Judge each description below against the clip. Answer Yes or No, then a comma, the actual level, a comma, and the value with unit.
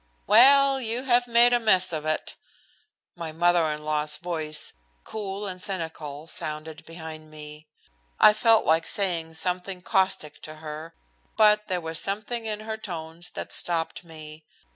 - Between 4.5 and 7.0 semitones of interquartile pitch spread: Yes, average, 5.1 semitones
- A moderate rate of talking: Yes, average, 150 wpm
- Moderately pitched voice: Yes, medium, 175 Hz